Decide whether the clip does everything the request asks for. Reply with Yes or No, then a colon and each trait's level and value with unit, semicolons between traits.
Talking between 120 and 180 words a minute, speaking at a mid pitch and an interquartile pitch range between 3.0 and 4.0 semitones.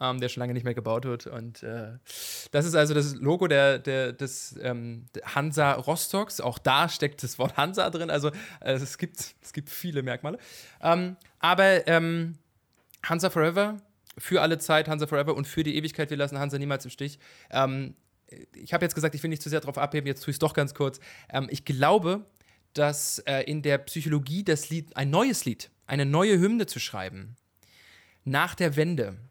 No: average, 195 wpm; medium, 145 Hz; average, 3.7 semitones